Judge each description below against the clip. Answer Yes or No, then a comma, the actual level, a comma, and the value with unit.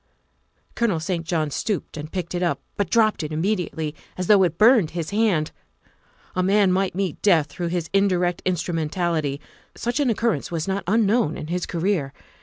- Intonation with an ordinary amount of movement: Yes, average, 3.7 semitones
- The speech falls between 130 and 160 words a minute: No, average, 180 wpm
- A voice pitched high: No, medium, 180 Hz